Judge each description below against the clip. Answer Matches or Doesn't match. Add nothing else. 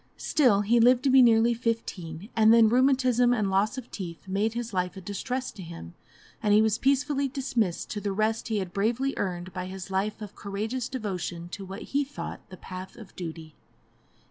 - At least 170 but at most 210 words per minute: Matches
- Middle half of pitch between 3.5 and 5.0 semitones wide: Matches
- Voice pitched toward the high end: Matches